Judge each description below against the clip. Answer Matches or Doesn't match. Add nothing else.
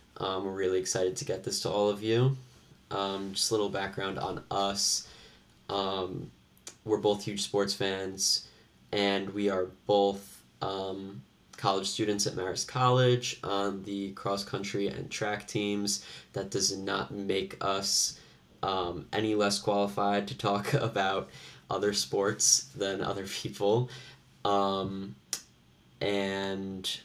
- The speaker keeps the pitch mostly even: Matches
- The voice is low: Matches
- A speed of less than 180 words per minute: Matches